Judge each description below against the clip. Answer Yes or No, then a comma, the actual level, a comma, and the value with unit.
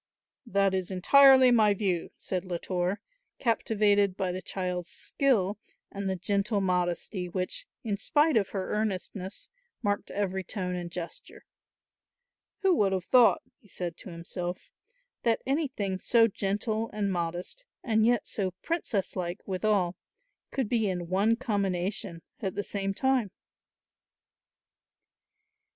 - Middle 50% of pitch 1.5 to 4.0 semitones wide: Yes, average, 3.3 semitones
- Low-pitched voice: No, high, 200 Hz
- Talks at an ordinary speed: No, slow, 130 wpm